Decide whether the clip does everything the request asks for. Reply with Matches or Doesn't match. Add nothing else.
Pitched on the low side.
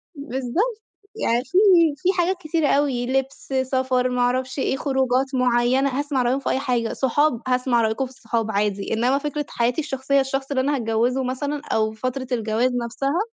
Doesn't match